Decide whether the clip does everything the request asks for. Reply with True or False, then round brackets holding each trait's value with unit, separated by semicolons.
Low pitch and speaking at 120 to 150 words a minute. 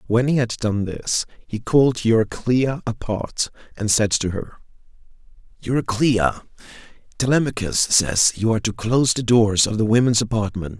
True (110 Hz; 145 wpm)